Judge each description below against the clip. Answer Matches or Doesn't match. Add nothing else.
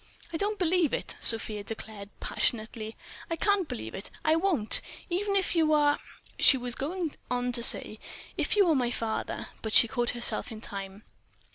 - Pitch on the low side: Doesn't match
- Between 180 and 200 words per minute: Doesn't match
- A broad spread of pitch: Matches